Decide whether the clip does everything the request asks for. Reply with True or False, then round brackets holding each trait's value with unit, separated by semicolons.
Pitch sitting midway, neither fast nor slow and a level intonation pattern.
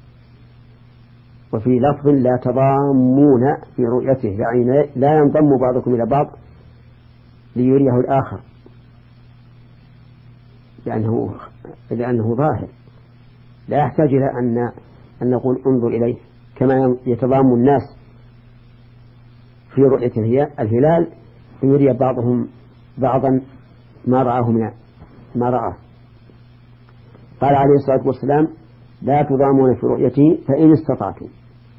False (125 Hz; 95 wpm; 1.8 semitones)